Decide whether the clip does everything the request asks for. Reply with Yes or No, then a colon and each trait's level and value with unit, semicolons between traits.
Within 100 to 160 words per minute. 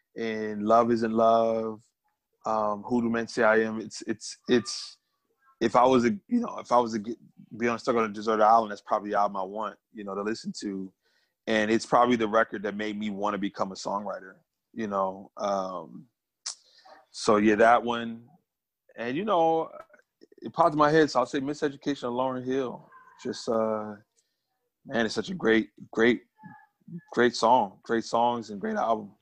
No: average, 185 wpm